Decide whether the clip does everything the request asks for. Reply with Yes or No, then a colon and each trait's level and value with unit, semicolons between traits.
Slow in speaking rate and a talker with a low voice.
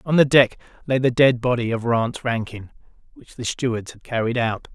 No: average, 200 wpm; low, 120 Hz